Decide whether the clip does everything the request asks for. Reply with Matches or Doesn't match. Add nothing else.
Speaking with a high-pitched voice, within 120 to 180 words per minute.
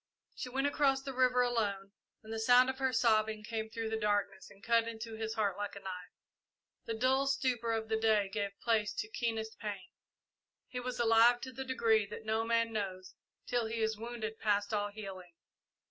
Doesn't match